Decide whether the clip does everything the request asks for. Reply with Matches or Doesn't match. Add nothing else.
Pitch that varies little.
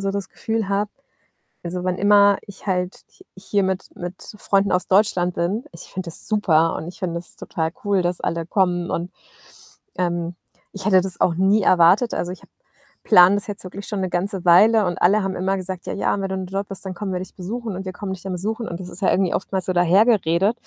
Matches